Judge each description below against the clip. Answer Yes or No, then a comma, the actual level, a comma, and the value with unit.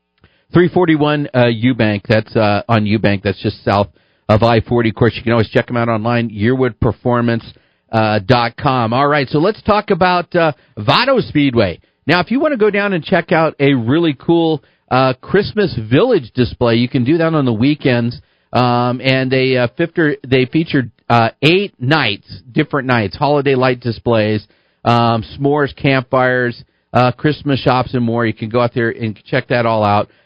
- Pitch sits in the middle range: No, low, 125 Hz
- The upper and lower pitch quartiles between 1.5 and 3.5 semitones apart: No, average, 4.2 semitones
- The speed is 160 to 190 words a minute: Yes, average, 180 wpm